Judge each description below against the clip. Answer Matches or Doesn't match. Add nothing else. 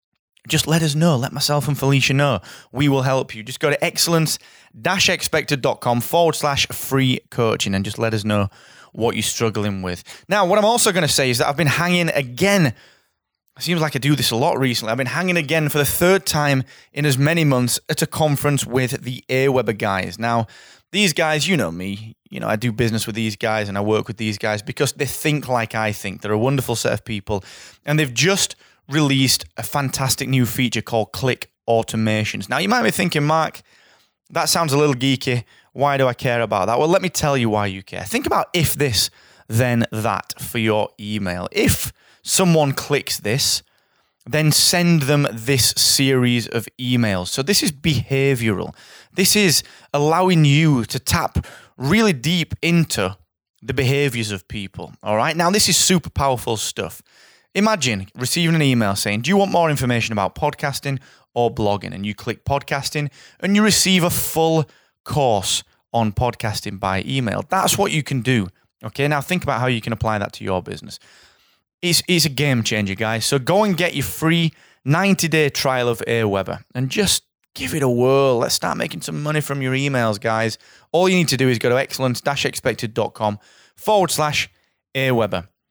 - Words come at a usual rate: Matches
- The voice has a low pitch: Matches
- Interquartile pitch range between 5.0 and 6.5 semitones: Matches